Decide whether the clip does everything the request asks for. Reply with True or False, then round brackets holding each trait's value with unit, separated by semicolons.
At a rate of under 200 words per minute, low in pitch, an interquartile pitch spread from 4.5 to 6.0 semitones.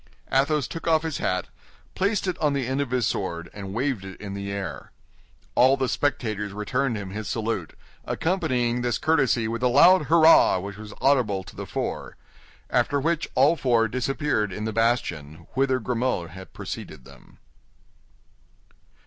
True (165 wpm; 120 Hz; 5.6 semitones)